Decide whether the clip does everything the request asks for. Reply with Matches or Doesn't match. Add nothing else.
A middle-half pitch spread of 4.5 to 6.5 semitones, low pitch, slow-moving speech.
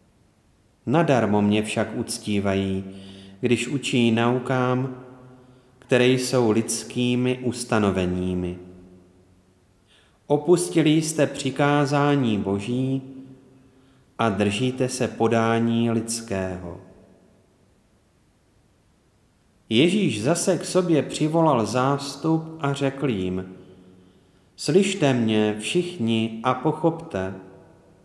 Matches